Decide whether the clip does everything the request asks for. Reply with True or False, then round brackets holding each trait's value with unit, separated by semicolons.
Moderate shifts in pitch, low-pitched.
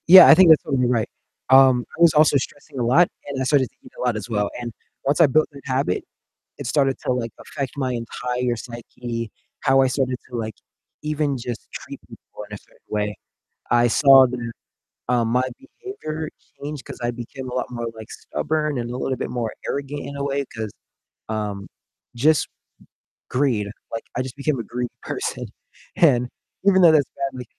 True (3.1 semitones; 130 Hz)